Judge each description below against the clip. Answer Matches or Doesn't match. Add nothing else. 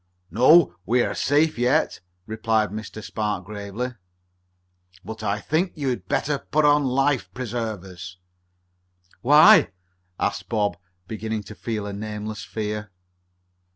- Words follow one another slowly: Matches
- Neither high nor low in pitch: Doesn't match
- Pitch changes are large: Doesn't match